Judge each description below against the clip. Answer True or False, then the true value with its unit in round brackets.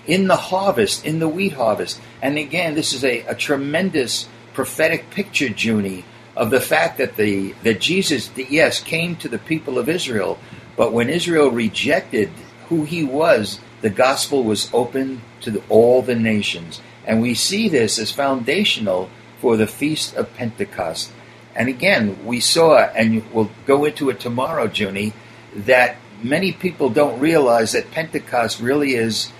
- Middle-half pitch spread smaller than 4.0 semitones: False (5.5 semitones)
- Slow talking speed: False (160 wpm)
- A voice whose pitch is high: False (130 Hz)